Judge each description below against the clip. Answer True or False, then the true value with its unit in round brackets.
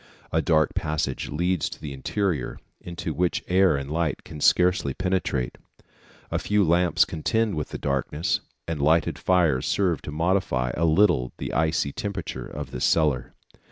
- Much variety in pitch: False (3.8 semitones)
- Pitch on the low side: True (80 Hz)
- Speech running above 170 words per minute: False (155 wpm)